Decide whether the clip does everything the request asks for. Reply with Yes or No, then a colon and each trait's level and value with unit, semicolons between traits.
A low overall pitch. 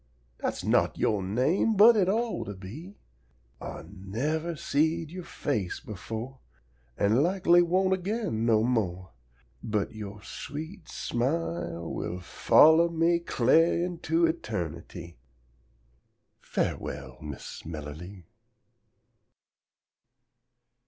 Yes: low, 130 Hz